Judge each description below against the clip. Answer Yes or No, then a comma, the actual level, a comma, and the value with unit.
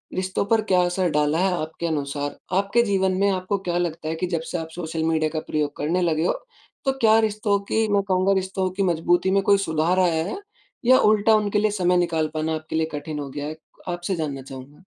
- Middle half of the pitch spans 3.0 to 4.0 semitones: Yes, average, 3.6 semitones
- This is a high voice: No, medium, 175 Hz